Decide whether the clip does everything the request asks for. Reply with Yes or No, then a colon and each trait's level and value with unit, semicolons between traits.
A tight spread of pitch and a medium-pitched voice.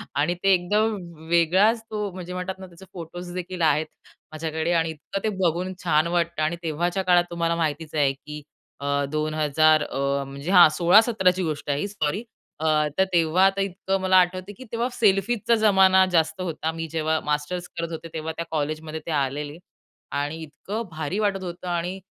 No: average, 3.3 semitones; medium, 170 Hz